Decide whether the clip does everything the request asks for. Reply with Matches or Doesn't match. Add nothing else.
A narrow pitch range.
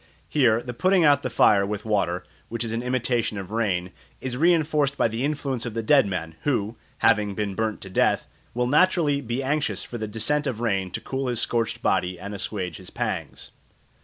Doesn't match